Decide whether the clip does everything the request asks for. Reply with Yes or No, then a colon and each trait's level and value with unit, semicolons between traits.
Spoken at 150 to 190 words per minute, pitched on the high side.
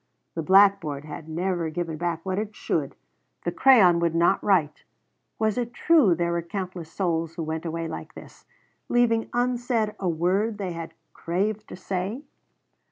No: average, 165 wpm; medium, 180 Hz